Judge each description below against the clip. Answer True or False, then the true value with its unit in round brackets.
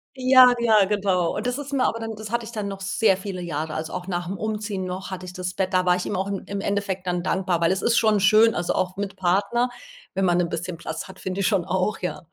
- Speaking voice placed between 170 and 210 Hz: True (190 Hz)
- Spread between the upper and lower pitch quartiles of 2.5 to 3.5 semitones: True (2.9 semitones)